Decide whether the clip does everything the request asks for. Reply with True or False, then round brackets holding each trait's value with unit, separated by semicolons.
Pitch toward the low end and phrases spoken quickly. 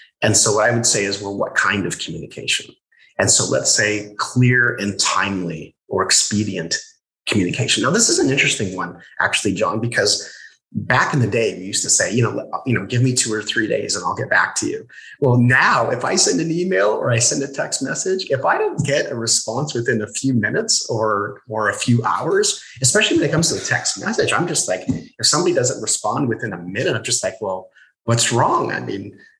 True (115 Hz; 220 wpm)